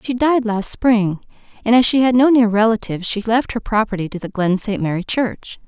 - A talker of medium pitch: No, high, 220 Hz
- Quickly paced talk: Yes, fast, 220 wpm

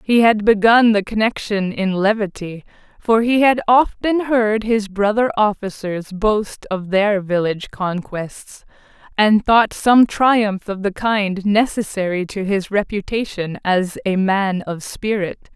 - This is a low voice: No, high, 205 Hz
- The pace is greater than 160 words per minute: No, average, 140 wpm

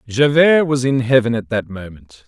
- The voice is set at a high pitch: No, low, 120 Hz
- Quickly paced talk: No, average, 185 wpm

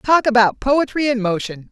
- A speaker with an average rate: Yes, average, 175 wpm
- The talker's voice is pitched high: Yes, high, 240 Hz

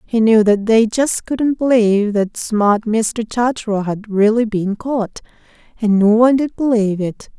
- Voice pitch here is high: Yes, high, 220 Hz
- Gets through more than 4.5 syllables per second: No, 4.4 syllables/s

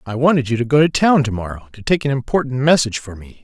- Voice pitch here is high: No, low, 130 Hz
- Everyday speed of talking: No, fast, 280 wpm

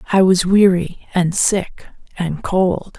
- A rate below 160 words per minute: Yes, average, 140 wpm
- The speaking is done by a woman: Yes, female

